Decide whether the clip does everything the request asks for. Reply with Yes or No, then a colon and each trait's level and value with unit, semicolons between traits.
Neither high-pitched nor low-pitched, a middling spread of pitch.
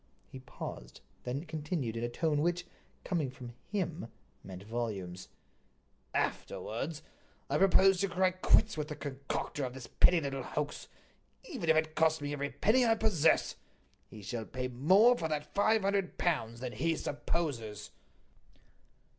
No: medium, 150 Hz; wide, 6.0 semitones